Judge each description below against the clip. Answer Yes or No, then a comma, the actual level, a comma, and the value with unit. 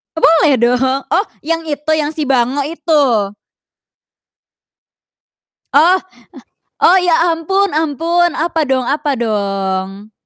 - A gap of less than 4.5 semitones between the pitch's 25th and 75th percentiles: No, wide, 5.5 semitones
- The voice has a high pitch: Yes, very high, 300 Hz